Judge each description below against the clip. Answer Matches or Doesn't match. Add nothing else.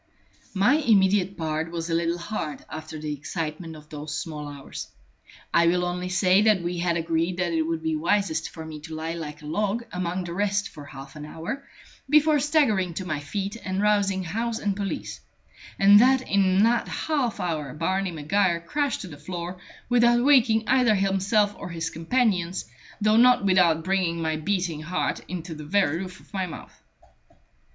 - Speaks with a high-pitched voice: Doesn't match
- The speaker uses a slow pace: Doesn't match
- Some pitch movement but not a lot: Matches